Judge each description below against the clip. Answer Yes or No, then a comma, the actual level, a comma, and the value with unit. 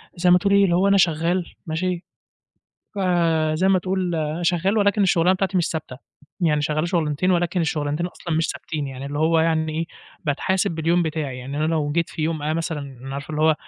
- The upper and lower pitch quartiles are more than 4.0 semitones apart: No, average, 2.7 semitones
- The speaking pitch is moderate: Yes, medium, 165 Hz